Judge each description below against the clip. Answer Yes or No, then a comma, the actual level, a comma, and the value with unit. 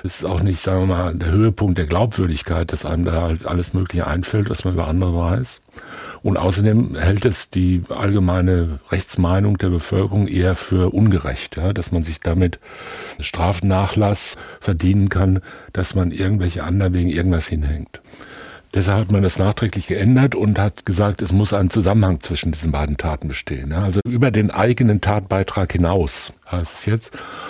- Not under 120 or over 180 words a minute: Yes, average, 170 wpm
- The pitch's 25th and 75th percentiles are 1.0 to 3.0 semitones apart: Yes, average, 2.7 semitones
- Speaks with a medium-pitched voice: No, very low, 95 Hz